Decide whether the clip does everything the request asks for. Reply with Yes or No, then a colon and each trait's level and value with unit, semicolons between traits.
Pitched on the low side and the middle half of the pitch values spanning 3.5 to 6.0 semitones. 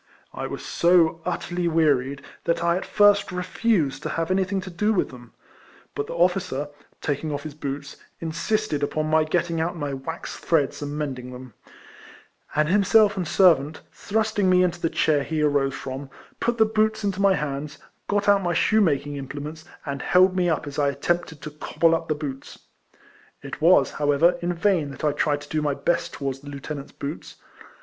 No: medium, 160 Hz; average, 4.1 semitones